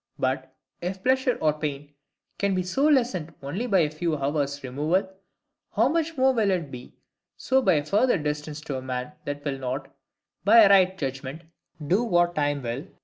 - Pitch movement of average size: No, wide, 5.9 semitones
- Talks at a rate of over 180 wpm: Yes, average, 190 wpm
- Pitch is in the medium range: Yes, medium, 155 Hz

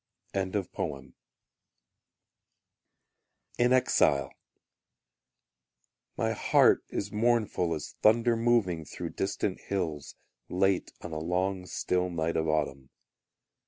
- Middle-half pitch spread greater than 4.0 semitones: Yes, average, 4.6 semitones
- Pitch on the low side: Yes, very low, 90 Hz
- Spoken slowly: Yes, slow, 90 wpm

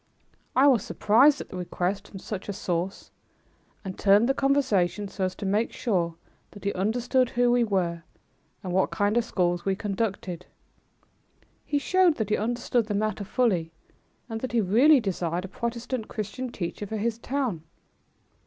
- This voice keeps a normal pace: Yes, average, 170 wpm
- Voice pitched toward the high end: Yes, high, 210 Hz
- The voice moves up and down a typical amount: Yes, average, 4.2 semitones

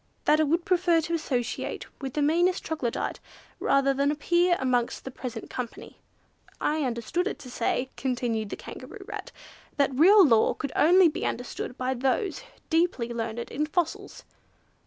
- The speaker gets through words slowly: No, average, 155 wpm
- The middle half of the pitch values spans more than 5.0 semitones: Yes, wide, 5.4 semitones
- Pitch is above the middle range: Yes, very high, 280 Hz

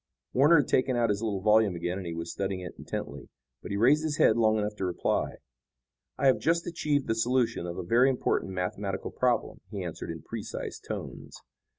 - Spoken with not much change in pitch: No, wide, 5.5 semitones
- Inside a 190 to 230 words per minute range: Yes, average, 200 wpm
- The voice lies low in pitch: Yes, low, 110 Hz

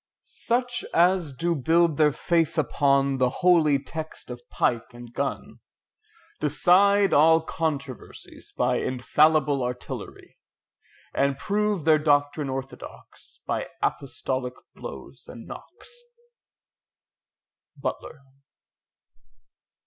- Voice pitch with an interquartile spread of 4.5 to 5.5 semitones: No, average, 4.0 semitones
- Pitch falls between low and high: Yes, medium, 150 Hz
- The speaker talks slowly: Yes, slow, 95 wpm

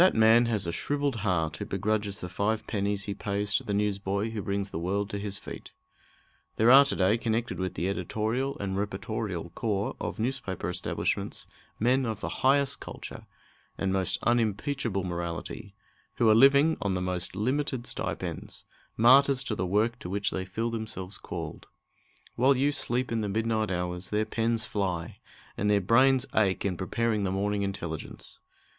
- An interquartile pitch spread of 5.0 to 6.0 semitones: No, average, 3.3 semitones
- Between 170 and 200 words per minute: Yes, average, 175 wpm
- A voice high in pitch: No, low, 105 Hz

